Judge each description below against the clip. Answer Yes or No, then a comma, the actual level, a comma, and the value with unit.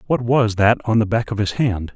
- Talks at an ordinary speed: No, fast, 275 wpm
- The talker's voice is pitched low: Yes, low, 110 Hz